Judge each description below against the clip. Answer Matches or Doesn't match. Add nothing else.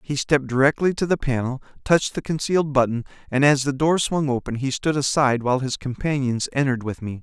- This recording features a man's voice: Matches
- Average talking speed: Doesn't match